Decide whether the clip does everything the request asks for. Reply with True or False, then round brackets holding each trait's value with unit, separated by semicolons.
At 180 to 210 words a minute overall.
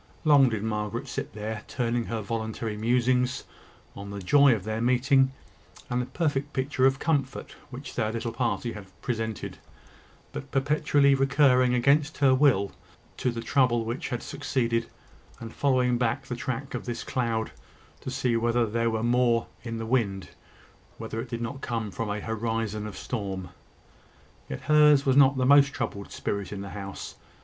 False (170 wpm)